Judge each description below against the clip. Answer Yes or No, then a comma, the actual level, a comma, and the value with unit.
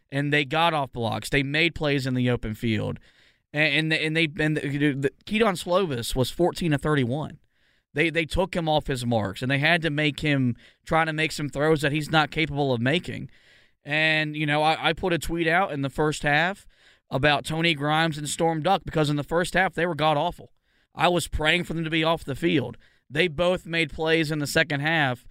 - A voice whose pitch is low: No, medium, 155 Hz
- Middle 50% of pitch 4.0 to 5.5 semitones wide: No, average, 2.7 semitones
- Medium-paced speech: No, fast, 220 wpm